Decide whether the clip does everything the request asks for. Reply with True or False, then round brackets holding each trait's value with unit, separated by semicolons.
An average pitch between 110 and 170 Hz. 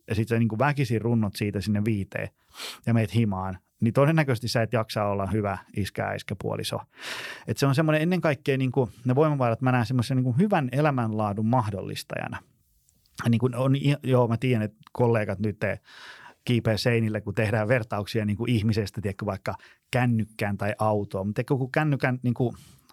True (115 Hz)